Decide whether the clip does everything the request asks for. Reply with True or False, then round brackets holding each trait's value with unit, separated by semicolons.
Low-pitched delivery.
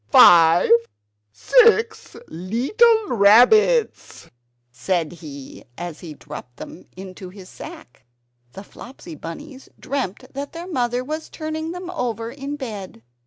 False (240 Hz)